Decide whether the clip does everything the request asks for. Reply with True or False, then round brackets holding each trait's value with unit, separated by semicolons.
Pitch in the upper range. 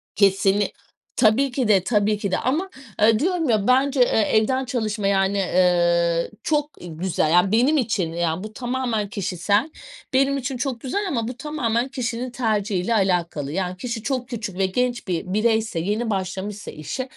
True (215 Hz)